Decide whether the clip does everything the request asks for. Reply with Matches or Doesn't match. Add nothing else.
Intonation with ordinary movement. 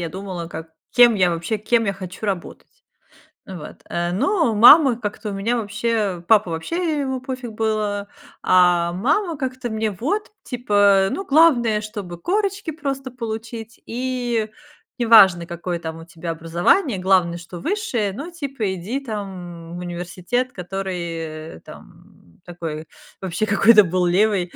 Doesn't match